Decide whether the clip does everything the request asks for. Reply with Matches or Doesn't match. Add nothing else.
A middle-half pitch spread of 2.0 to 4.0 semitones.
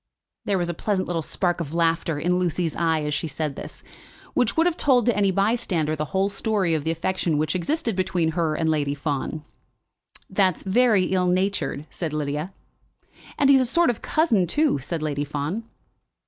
Doesn't match